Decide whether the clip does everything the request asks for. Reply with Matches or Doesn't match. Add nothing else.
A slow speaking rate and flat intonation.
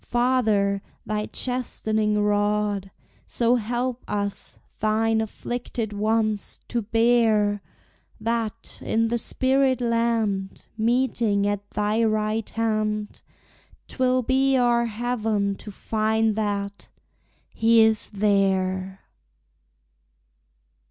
Matches